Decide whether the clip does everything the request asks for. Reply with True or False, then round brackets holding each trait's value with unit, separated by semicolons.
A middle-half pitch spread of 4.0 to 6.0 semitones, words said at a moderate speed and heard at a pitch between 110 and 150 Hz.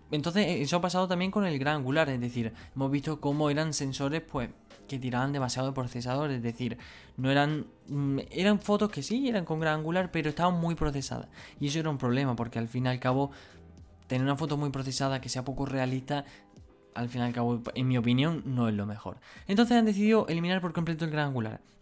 False (4.5 semitones; 215 wpm; 140 Hz)